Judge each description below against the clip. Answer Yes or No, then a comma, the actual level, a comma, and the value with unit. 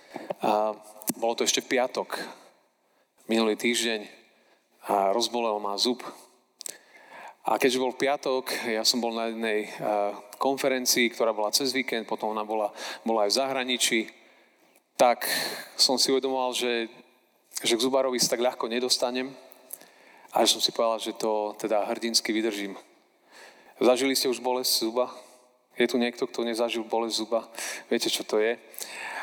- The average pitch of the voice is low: Yes, low, 120 Hz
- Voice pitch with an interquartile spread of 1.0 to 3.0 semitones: Yes, narrow, 2.4 semitones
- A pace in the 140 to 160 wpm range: Yes, average, 145 wpm